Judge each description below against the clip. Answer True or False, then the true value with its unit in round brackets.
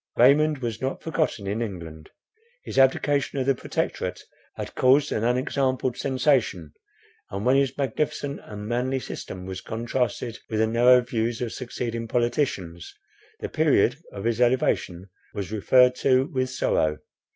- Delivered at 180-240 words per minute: False (145 wpm)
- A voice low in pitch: True (120 Hz)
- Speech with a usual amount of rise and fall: True (3.3 semitones)